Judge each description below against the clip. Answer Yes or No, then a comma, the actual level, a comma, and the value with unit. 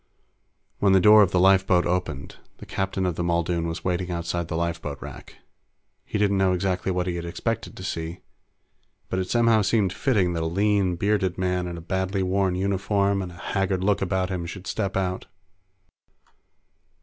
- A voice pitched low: Yes, very low, 95 Hz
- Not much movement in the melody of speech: Yes, narrow, 2.0 semitones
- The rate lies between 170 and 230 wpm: Yes, average, 185 wpm